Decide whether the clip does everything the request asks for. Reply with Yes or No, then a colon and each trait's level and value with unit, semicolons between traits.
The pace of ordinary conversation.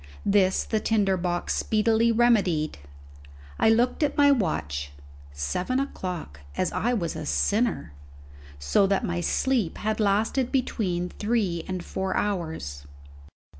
No: slow, 130 wpm